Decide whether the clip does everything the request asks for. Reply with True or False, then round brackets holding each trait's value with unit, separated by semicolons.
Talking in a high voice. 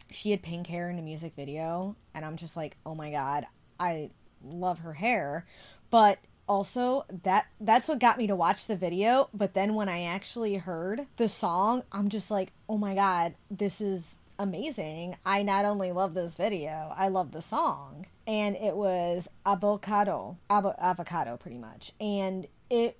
True (195 Hz)